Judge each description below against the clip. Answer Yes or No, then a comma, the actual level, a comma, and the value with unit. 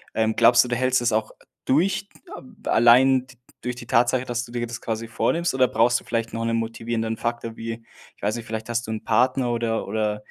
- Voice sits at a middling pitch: No, low, 120 Hz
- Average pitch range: No, narrow, 1.6 semitones